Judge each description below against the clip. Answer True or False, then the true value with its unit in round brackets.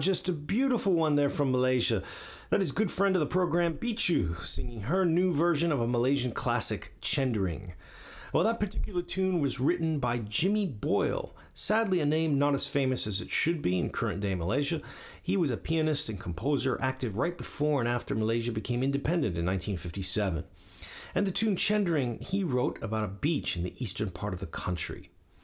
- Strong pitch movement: True (9.0 semitones)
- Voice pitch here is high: False (130 Hz)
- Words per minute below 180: False (185 wpm)